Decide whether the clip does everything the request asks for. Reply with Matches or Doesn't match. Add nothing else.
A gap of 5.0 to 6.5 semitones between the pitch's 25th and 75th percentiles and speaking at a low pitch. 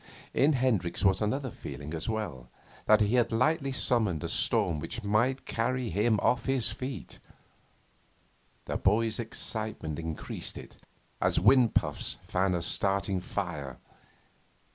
Matches